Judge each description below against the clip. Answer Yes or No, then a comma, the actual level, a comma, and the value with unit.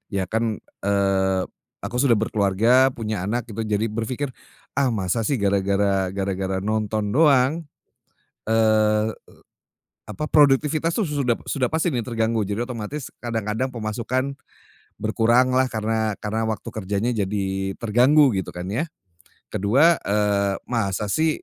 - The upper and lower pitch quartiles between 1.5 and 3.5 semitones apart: No, average, 4.0 semitones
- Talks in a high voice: No, low, 110 Hz